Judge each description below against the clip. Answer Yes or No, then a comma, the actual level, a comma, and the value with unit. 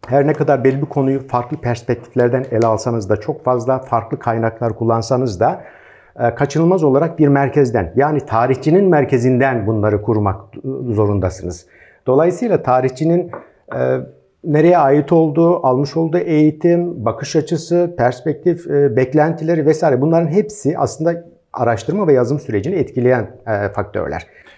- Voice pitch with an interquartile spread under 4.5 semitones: No, average, 5.1 semitones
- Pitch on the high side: No, low, 135 Hz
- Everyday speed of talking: Yes, average, 120 wpm